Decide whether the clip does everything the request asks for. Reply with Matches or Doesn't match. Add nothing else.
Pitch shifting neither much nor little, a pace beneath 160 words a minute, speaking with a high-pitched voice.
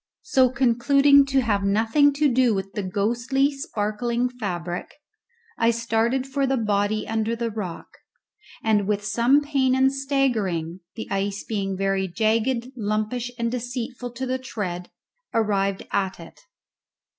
Matches